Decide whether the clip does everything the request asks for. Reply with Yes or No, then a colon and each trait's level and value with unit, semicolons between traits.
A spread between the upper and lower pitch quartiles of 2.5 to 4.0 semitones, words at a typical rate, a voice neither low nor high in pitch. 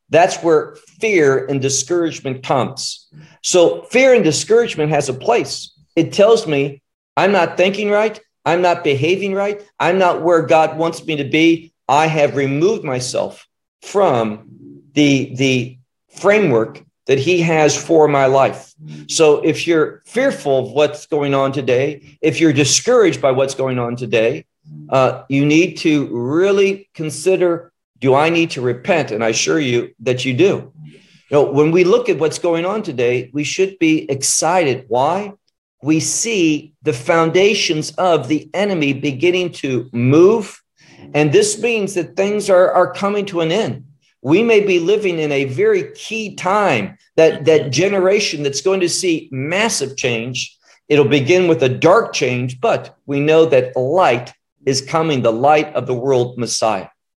No: average, 5.3 semitones; average, 160 wpm; medium, 155 Hz